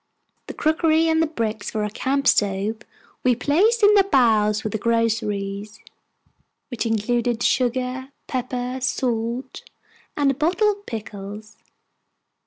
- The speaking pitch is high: Yes, high, 245 Hz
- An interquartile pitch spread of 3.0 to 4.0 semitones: No, average, 4.5 semitones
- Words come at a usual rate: No, slow, 130 wpm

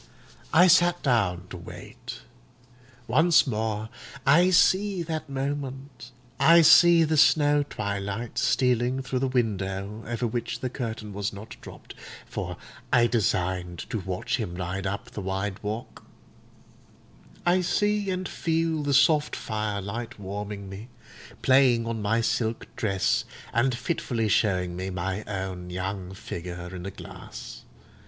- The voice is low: Yes, low, 115 Hz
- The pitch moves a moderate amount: No, wide, 6.0 semitones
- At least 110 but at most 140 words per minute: Yes, slow, 135 wpm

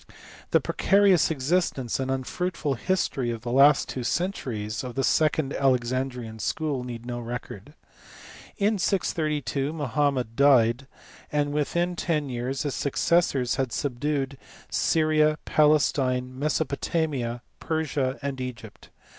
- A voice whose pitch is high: No, low, 135 Hz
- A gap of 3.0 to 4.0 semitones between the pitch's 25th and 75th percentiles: Yes, average, 3.6 semitones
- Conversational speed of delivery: No, slow, 115 wpm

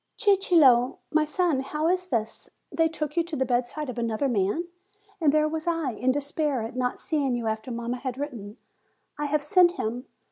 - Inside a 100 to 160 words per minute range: No, average, 190 wpm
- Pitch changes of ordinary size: Yes, average, 4.5 semitones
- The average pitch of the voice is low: No, very high, 280 Hz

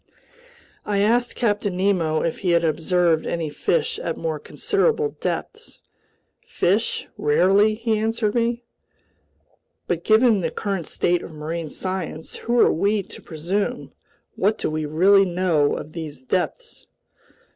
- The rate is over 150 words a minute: No, slow, 135 wpm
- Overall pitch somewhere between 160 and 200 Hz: Yes, high, 190 Hz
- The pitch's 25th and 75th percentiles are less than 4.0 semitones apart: No, average, 5.1 semitones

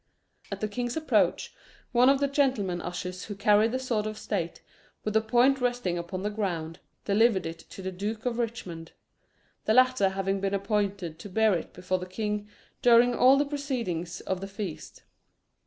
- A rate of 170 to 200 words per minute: Yes, average, 180 wpm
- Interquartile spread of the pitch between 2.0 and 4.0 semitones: No, average, 4.6 semitones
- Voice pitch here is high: Yes, high, 210 Hz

